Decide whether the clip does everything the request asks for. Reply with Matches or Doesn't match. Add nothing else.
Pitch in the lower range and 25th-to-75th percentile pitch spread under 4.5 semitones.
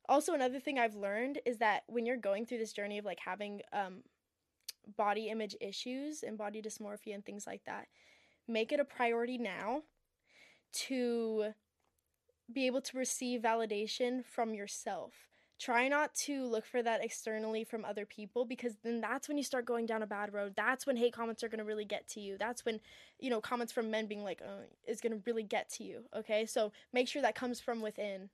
Doesn't match